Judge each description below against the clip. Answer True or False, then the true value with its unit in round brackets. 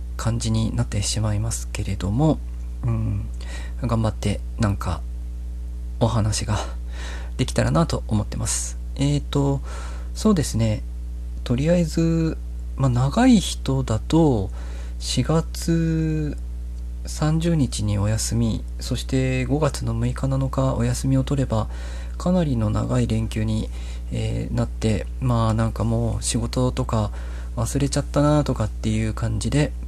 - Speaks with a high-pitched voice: False (110 Hz)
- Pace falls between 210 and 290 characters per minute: True (245 characters per minute)